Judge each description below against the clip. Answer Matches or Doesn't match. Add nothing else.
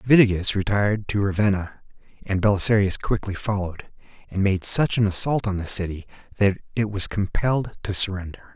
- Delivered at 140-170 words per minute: Matches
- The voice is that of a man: Matches